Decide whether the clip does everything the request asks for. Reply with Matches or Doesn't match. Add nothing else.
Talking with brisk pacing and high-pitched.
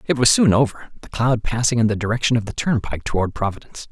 Doesn't match